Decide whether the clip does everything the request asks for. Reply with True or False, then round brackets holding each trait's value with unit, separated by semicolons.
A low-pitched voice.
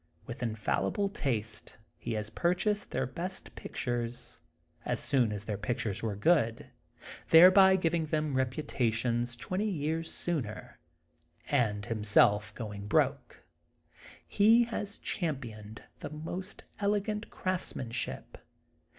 True (130 Hz)